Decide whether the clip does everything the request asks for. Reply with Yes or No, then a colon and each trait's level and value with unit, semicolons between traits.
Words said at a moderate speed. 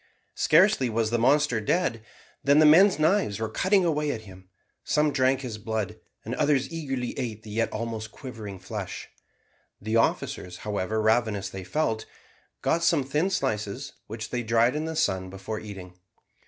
Yes: average, 165 wpm